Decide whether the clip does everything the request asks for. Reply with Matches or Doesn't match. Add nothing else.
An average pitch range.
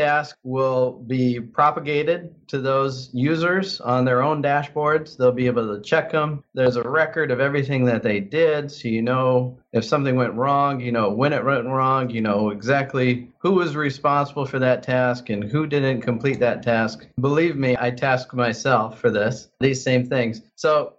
Matches